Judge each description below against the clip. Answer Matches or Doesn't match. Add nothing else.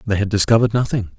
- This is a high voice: Doesn't match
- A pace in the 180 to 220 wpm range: Matches